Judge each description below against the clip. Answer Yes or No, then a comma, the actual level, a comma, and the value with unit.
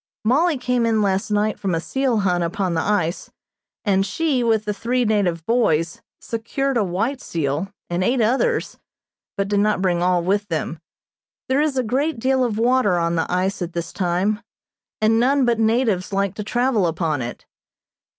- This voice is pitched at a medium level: No, high, 210 Hz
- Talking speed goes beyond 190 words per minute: No, average, 180 wpm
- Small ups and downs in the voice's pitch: No, average, 5.2 semitones